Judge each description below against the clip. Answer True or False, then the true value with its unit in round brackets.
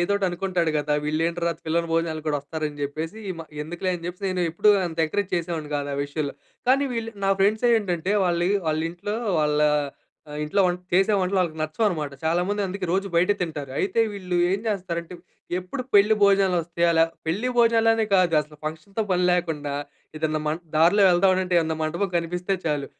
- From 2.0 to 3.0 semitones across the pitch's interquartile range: False (3.6 semitones)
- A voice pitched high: False (175 Hz)